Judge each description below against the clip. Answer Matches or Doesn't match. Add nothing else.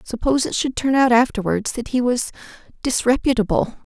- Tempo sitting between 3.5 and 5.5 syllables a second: Doesn't match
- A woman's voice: Matches